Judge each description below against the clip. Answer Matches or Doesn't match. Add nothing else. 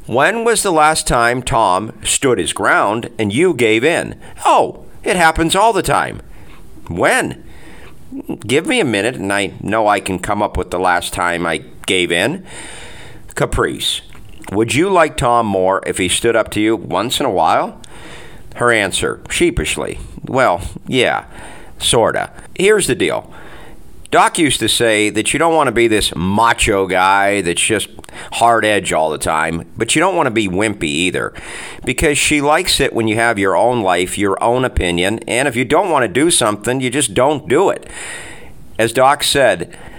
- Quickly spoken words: Doesn't match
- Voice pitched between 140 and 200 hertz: Doesn't match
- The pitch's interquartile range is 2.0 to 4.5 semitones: Doesn't match